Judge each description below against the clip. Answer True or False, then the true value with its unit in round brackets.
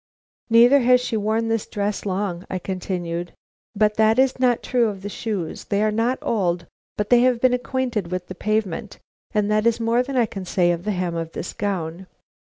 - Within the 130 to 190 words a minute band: False (205 wpm)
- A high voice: True (210 Hz)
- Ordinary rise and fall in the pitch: True (4.0 semitones)